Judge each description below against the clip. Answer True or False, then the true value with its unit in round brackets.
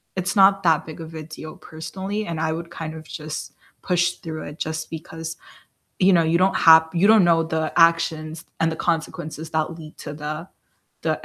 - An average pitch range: False (1.5 semitones)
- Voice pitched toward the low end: False (160 Hz)